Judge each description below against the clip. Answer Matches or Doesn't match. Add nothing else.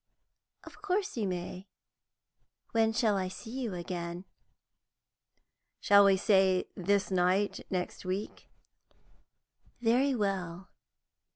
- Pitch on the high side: Matches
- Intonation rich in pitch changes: Doesn't match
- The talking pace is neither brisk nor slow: Doesn't match